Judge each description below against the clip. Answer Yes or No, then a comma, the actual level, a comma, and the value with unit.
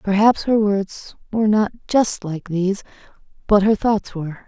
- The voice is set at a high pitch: Yes, high, 205 Hz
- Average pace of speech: Yes, average, 160 wpm